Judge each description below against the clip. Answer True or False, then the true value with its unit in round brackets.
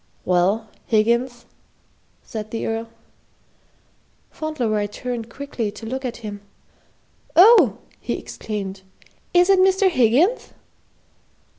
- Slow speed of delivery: True (100 wpm)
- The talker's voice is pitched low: False (235 Hz)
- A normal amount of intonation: False (6.2 semitones)